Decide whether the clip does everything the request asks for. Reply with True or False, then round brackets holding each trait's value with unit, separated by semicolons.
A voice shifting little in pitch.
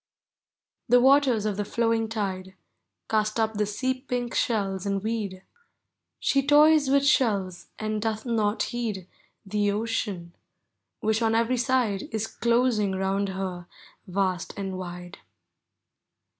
False (3.4 semitones)